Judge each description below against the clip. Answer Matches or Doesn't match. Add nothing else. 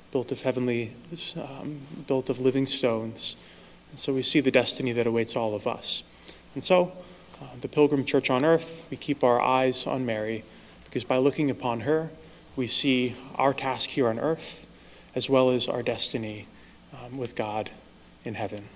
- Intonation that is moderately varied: Matches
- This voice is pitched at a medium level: Doesn't match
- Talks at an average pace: Matches